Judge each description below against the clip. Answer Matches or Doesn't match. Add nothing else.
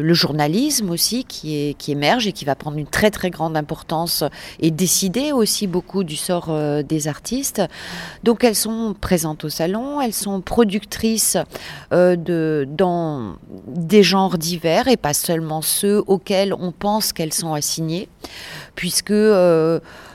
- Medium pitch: Matches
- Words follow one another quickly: Doesn't match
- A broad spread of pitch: Doesn't match